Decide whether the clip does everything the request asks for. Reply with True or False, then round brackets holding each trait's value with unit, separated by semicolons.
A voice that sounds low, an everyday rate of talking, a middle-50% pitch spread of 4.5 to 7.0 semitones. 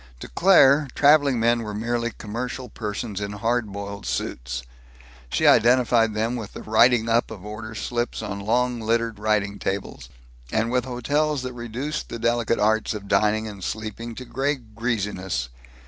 False (115 Hz; 160 wpm; 2.7 semitones)